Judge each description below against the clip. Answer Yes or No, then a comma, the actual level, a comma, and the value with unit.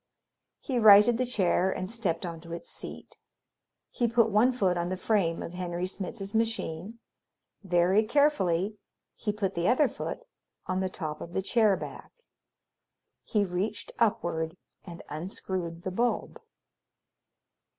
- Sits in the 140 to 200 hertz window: Yes, high, 190 Hz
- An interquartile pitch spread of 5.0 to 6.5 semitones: No, average, 4.2 semitones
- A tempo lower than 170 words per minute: Yes, average, 140 wpm